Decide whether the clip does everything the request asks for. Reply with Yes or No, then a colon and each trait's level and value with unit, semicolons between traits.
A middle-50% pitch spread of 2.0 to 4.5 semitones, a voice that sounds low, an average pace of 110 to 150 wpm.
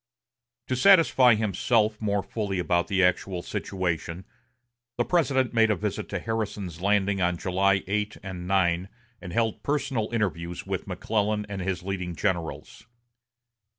Yes: average, 3.5 semitones; low, 100 Hz; average, 140 wpm